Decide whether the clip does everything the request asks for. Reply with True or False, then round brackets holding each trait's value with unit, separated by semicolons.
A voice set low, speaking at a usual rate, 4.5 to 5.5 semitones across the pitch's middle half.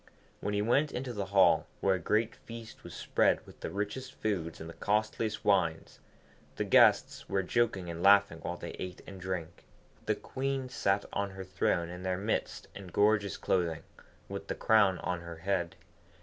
False (100 Hz; 180 wpm; 3.3 semitones)